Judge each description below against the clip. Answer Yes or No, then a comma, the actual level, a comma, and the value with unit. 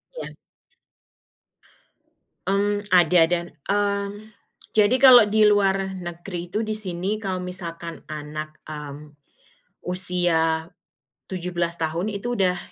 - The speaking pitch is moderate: Yes, medium, 180 Hz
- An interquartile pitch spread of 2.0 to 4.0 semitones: Yes, average, 3.3 semitones